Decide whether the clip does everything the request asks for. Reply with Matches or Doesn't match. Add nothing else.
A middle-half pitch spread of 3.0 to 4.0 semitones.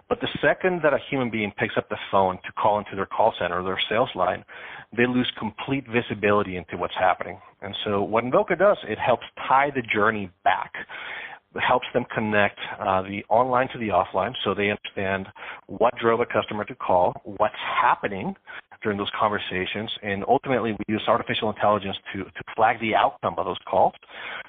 Matches